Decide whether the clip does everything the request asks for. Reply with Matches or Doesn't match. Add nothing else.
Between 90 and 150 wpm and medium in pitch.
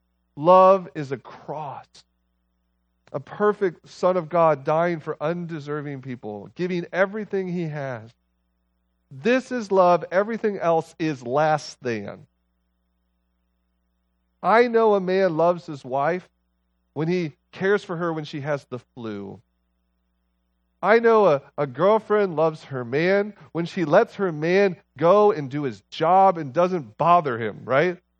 Matches